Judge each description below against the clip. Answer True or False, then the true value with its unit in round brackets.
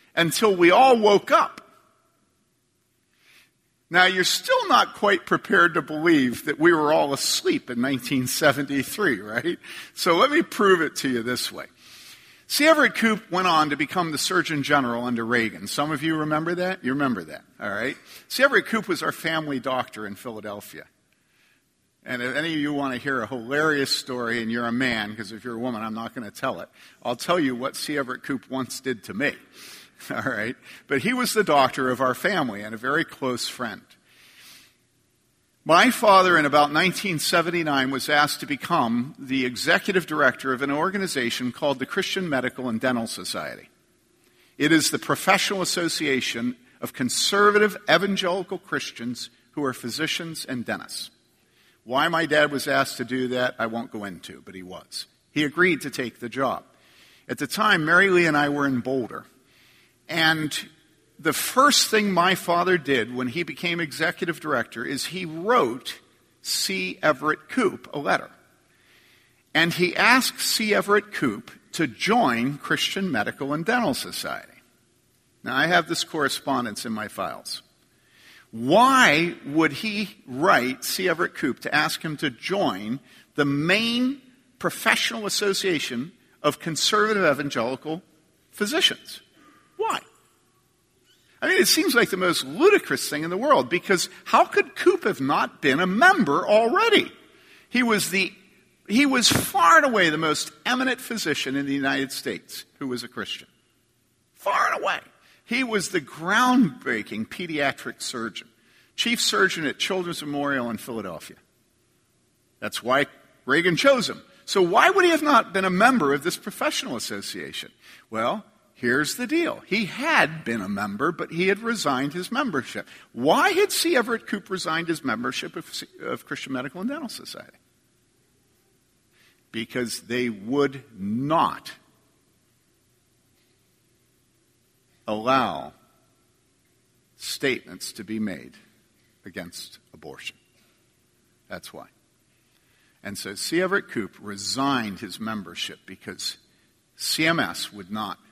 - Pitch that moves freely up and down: True (8.1 semitones)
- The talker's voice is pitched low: False (155 Hz)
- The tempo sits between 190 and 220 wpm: False (150 wpm)